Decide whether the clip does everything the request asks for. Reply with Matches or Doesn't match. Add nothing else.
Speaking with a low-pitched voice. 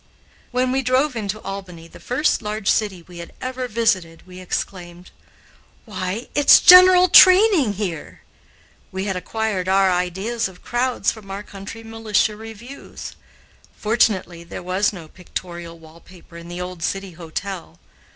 Doesn't match